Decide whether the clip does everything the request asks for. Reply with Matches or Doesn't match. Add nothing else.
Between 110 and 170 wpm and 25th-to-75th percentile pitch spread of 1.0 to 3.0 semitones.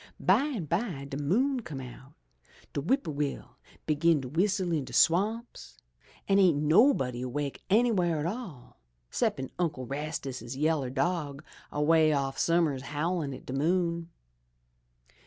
Doesn't match